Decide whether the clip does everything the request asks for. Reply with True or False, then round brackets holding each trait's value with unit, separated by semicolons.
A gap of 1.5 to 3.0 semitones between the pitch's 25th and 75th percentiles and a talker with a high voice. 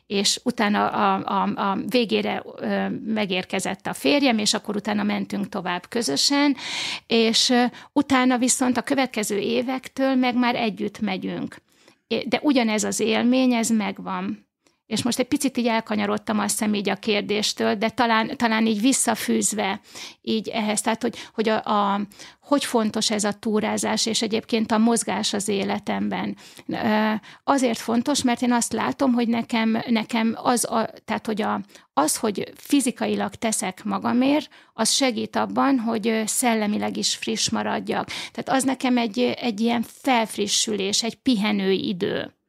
True (2.6 semitones; 225 Hz)